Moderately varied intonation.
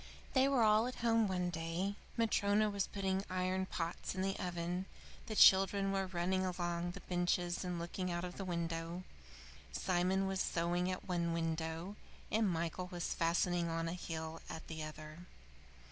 No: narrow, 2.2 semitones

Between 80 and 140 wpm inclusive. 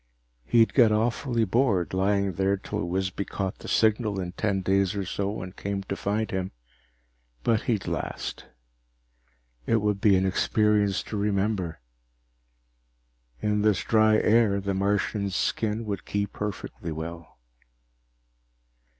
Yes: slow, 135 wpm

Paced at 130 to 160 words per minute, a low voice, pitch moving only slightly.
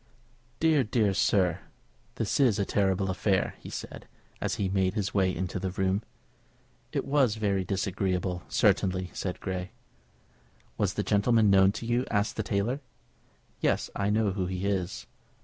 Yes: average, 155 wpm; low, 100 Hz; narrow, 2.3 semitones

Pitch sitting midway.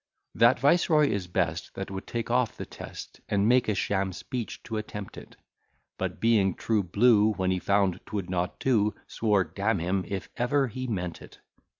No: low, 105 Hz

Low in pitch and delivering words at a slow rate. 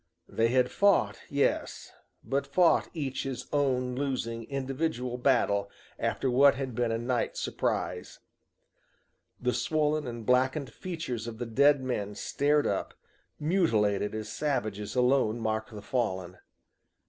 Yes: low, 125 Hz; slow, 130 wpm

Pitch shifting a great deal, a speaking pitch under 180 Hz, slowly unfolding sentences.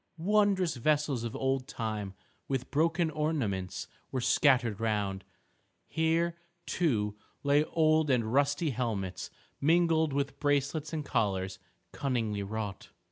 Yes: wide, 6.2 semitones; medium, 140 Hz; slow, 115 wpm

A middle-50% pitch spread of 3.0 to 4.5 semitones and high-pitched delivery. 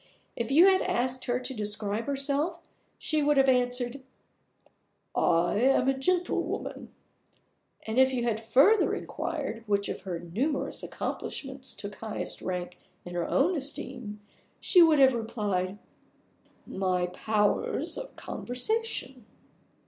No: average, 5.0 semitones; high, 245 Hz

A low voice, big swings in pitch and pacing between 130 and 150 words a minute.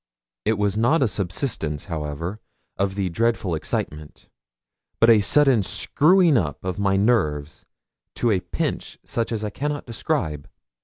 Yes: low, 100 Hz; wide, 5.8 semitones; average, 145 wpm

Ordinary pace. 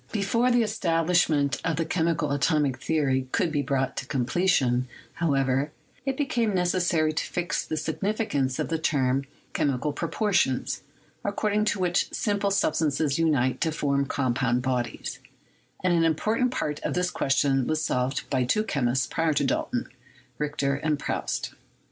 Yes: average, 155 wpm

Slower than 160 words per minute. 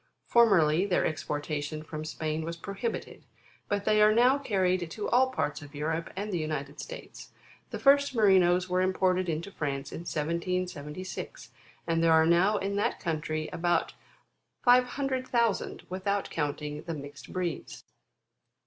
Yes: average, 140 wpm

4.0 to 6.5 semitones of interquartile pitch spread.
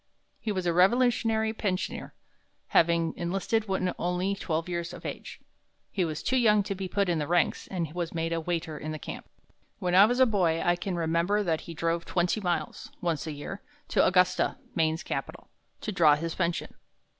No: average, 3.0 semitones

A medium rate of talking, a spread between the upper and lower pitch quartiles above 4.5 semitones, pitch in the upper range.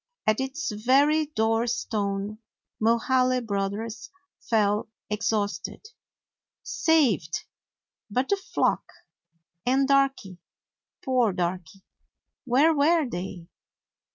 No: slow, 95 wpm; average, 5.1 semitones; high, 230 Hz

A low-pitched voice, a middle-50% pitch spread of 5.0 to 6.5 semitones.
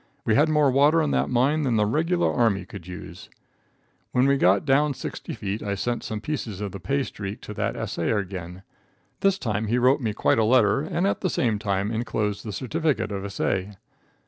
Yes: low, 115 Hz; wide, 5.5 semitones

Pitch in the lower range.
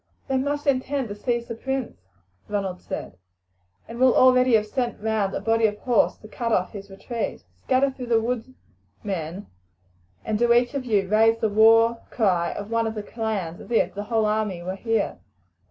No: high, 225 Hz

